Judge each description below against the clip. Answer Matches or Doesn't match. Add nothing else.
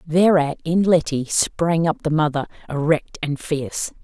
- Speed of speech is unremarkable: Matches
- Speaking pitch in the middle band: Matches